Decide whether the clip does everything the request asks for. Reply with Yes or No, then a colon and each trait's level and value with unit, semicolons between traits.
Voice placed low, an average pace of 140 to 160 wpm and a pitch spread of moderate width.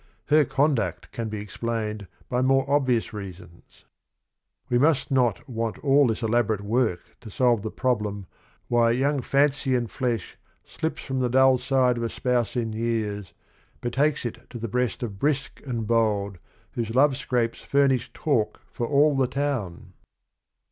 Yes: low, 120 Hz; average, 155 wpm; average, 3.4 semitones